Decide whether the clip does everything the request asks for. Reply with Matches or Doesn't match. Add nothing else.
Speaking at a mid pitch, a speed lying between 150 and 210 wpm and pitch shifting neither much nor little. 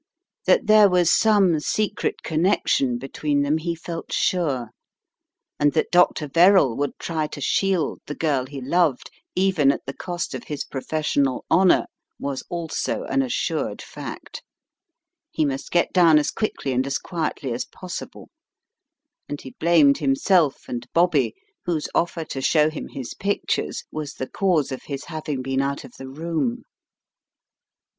Matches